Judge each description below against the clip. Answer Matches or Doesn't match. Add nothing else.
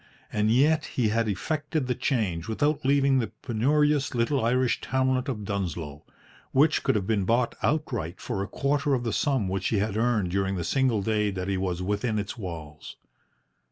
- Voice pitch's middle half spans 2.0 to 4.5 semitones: Doesn't match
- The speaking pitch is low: Matches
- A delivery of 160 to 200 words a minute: Matches